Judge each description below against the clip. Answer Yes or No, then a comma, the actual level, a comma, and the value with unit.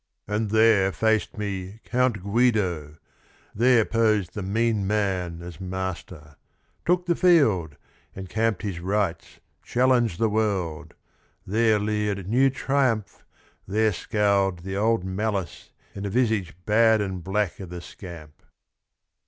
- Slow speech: Yes, slow, 130 wpm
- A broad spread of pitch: No, average, 3.2 semitones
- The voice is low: Yes, low, 105 Hz